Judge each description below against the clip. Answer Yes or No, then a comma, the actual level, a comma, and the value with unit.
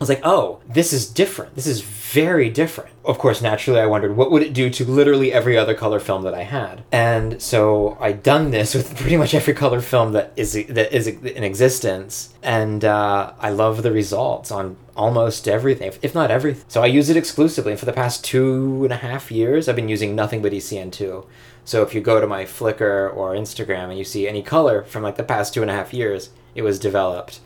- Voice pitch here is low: Yes, low, 115 Hz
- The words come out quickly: Yes, fast, 225 wpm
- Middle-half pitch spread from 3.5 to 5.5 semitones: Yes, average, 4.2 semitones